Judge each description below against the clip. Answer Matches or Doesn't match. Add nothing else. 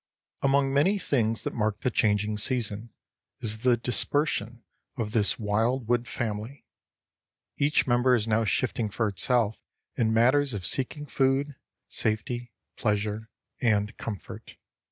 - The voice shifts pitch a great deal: Doesn't match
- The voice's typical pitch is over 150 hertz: Doesn't match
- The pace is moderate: Doesn't match